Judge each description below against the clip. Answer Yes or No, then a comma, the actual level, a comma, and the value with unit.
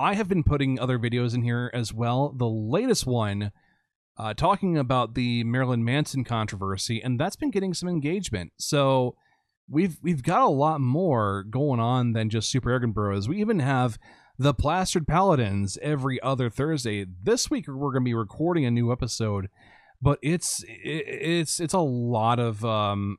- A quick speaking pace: No, average, 175 wpm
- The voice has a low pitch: Yes, low, 130 Hz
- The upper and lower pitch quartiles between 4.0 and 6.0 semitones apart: Yes, average, 5.2 semitones